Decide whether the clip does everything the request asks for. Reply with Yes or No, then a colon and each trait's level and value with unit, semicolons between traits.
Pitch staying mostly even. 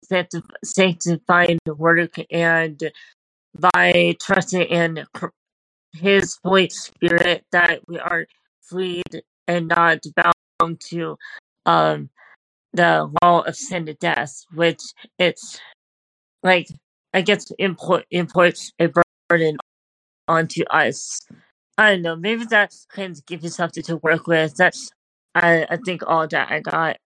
Yes: narrow, 1.9 semitones